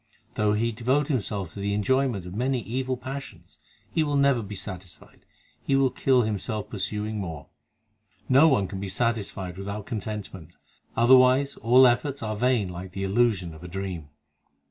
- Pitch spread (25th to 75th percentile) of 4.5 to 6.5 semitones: Yes, average, 4.8 semitones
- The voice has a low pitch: Yes, low, 110 Hz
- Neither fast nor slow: Yes, average, 165 wpm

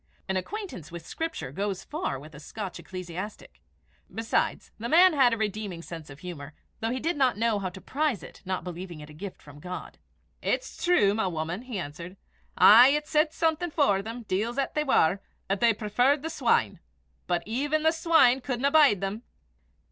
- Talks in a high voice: Yes, high, 215 Hz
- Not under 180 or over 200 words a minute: Yes, average, 190 wpm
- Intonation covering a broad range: Yes, wide, 7.7 semitones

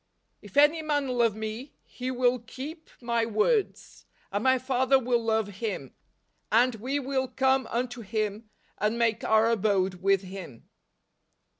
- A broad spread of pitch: No, average, 3.5 semitones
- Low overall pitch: No, high, 235 Hz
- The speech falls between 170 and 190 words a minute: No, average, 150 wpm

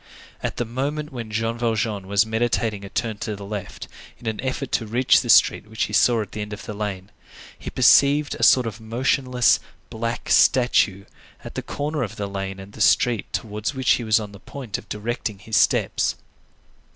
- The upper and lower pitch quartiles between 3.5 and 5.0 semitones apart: No, average, 2.9 semitones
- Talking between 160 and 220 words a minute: Yes, average, 200 wpm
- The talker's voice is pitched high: No, low, 110 Hz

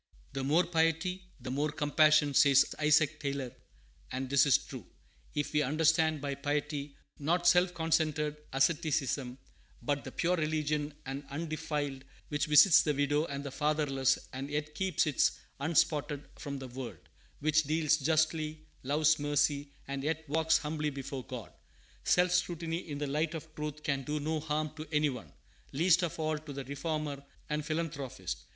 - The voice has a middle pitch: Yes, medium, 150 Hz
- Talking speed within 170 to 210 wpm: No, average, 160 wpm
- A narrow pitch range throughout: Yes, narrow, 1.9 semitones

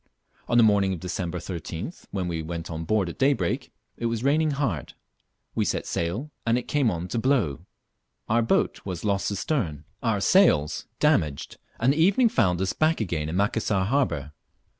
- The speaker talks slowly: No, average, 180 wpm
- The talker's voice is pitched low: Yes, low, 100 Hz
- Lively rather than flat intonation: Yes, wide, 6.7 semitones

